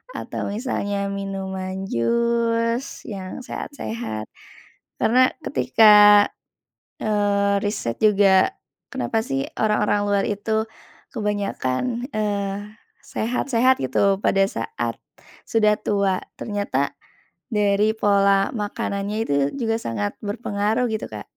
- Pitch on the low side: No, high, 205 Hz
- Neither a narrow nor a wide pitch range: No, narrow, 2.3 semitones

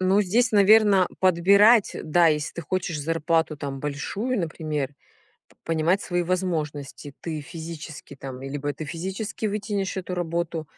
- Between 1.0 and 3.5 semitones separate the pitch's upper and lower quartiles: No, average, 4.1 semitones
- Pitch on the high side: No, medium, 170 Hz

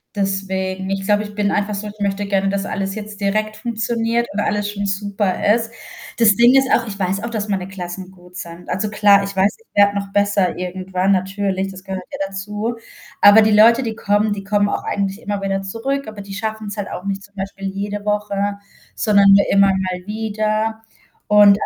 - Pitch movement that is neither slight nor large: No, narrow, 1.5 semitones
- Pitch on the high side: Yes, high, 200 Hz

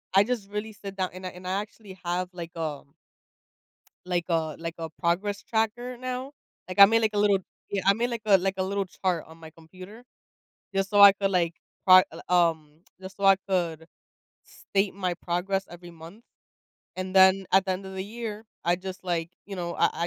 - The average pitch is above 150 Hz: Yes, high, 190 Hz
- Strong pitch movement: No, narrow, 2.6 semitones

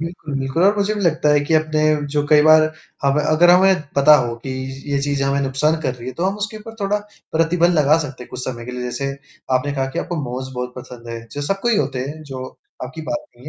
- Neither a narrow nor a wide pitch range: Yes, average, 4.2 semitones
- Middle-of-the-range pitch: Yes, medium, 145 Hz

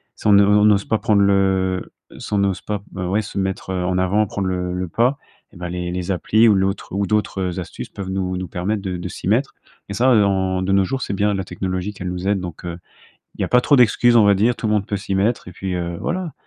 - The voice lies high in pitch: No, very low, 95 Hz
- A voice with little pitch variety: Yes, narrow, 2.3 semitones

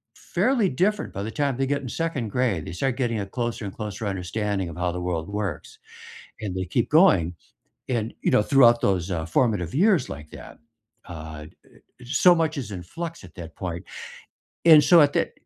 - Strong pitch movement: Yes, wide, 7.6 semitones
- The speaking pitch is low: Yes, low, 110 Hz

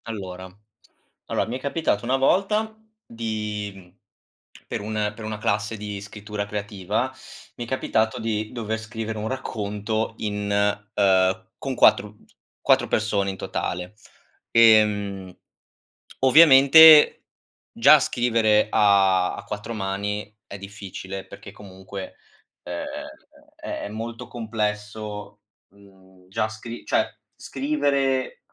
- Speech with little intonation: Yes, narrow, 2.3 semitones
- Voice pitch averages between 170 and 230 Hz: No, low, 105 Hz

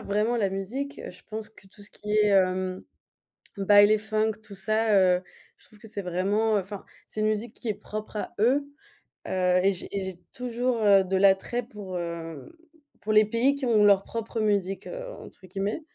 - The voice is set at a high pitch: Yes, high, 210 Hz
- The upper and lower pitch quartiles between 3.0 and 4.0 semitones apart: No, narrow, 2.4 semitones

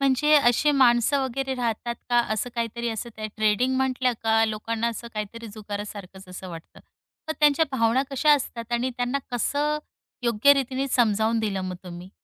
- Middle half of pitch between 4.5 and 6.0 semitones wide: No, average, 3.4 semitones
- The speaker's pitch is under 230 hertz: No, high, 235 Hz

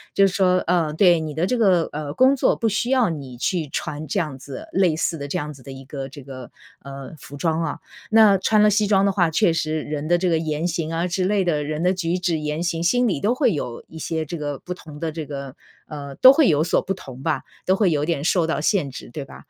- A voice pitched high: No, medium, 165 Hz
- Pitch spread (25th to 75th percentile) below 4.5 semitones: Yes, average, 4.1 semitones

